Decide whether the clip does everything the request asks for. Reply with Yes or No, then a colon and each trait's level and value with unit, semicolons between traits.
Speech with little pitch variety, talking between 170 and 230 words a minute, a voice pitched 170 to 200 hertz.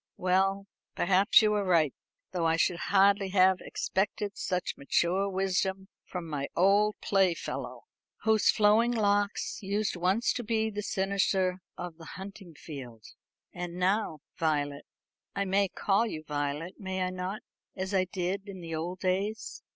No: narrow, 2.3 semitones; average, 150 wpm; high, 190 Hz